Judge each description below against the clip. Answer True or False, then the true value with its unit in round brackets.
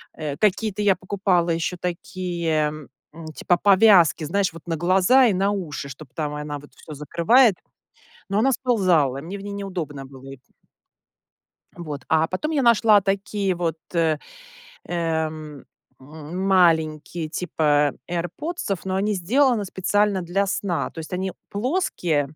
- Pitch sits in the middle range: True (175 Hz)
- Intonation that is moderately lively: True (4.2 semitones)